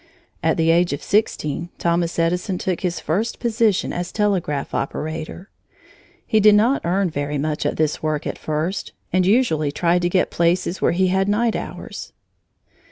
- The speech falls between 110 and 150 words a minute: No, average, 165 wpm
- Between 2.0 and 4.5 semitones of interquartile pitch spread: Yes, average, 3.9 semitones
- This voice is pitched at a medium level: Yes, medium, 175 Hz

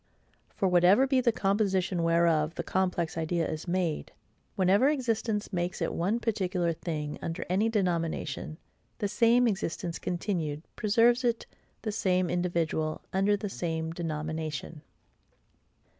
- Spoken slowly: Yes, slow, 130 wpm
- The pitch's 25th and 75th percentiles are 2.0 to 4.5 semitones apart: Yes, average, 4.0 semitones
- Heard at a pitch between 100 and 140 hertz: No, medium, 180 Hz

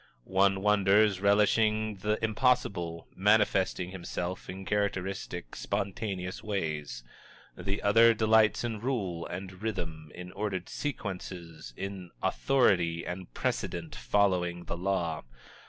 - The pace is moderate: No, slow, 105 wpm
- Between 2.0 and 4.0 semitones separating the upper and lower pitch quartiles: Yes, average, 3.1 semitones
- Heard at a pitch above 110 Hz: No, very low, 95 Hz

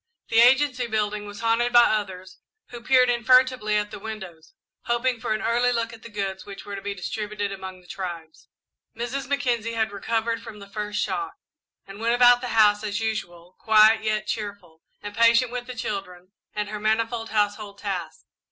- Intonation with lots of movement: No, narrow, 2.6 semitones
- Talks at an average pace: Yes, average, 190 wpm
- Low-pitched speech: No, high, 215 Hz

